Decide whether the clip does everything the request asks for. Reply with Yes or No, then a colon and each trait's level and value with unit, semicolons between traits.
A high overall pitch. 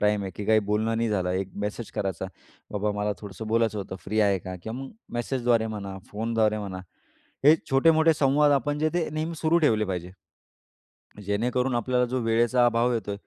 No: low, 110 Hz